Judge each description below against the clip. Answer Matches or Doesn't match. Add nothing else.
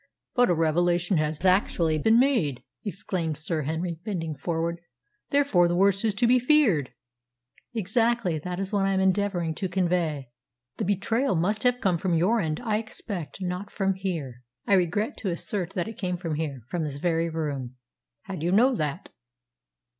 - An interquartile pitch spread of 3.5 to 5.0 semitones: Matches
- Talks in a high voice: Doesn't match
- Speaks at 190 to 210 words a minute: Doesn't match